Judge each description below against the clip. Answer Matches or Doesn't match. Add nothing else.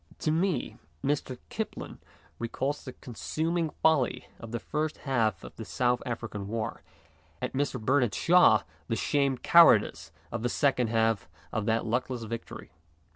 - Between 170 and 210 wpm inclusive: Doesn't match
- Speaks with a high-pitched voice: Doesn't match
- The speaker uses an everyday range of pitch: Matches